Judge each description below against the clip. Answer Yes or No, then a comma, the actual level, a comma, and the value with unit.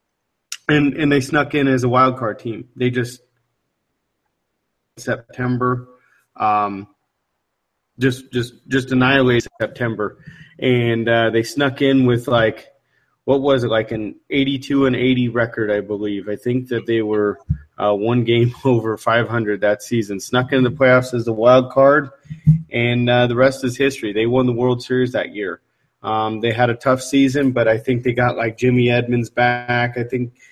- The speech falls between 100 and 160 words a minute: No, average, 175 wpm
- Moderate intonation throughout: No, narrow, 2.1 semitones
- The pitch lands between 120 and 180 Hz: Yes, low, 125 Hz